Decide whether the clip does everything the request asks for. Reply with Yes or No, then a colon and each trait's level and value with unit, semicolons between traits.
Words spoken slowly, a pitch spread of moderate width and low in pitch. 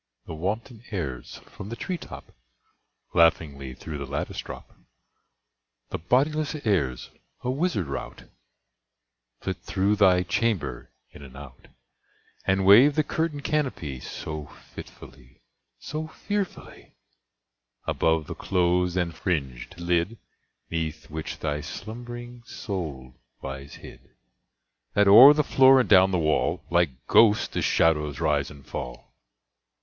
No: slow, 125 wpm; wide, 8.1 semitones; very low, 90 Hz